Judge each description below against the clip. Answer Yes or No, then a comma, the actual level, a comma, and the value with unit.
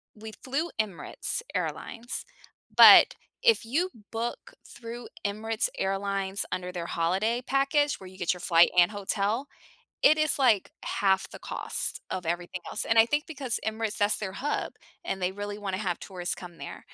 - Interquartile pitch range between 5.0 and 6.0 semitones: No, average, 4.2 semitones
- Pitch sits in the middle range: No, high, 205 Hz